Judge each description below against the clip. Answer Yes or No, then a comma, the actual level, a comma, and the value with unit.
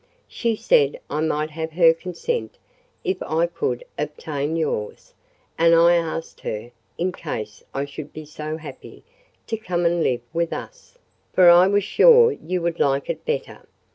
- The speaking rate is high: No, average, 160 wpm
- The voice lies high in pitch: No, medium, 165 Hz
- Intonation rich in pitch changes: No, average, 3.2 semitones